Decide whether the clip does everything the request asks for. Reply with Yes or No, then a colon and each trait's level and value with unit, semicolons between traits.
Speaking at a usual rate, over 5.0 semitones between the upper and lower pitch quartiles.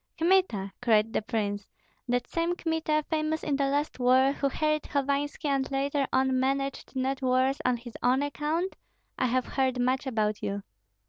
No: average, 170 wpm; average, 2.9 semitones